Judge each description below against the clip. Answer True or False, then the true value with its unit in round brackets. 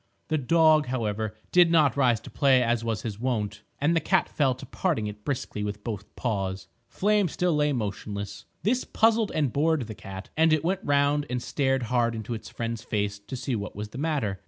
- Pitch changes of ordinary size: False (6.3 semitones)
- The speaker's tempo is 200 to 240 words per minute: True (205 wpm)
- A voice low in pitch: True (125 Hz)